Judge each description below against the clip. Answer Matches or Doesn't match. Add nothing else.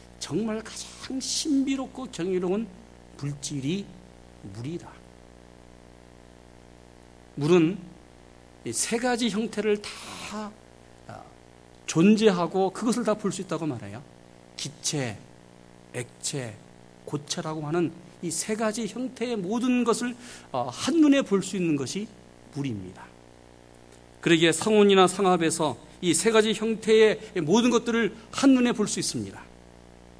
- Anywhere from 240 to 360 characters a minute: Doesn't match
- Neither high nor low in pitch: Matches